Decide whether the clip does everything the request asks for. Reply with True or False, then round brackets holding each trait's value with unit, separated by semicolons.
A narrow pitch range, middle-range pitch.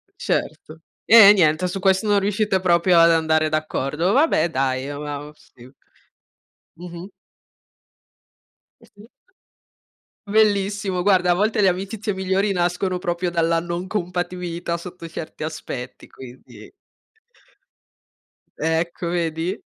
False (3.0 semitones; 175 Hz)